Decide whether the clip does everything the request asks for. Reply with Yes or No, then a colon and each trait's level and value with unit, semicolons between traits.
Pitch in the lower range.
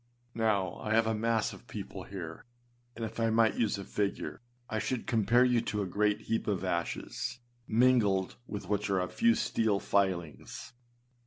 Yes: low, 105 Hz